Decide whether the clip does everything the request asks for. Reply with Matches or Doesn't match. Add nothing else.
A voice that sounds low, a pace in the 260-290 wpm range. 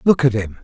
Matches